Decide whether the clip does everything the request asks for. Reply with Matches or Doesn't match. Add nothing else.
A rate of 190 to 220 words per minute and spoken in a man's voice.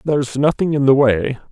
Matches